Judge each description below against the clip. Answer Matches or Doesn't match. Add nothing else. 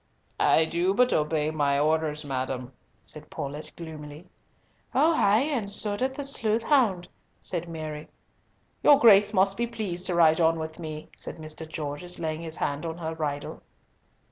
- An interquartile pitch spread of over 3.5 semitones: Matches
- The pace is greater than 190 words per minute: Doesn't match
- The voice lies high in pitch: Doesn't match